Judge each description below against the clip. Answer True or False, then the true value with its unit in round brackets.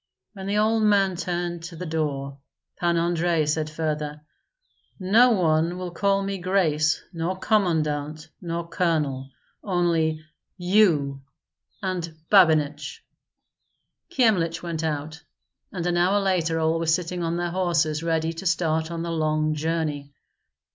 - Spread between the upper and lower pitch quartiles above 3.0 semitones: False (2.7 semitones)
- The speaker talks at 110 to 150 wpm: True (135 wpm)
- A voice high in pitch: False (165 Hz)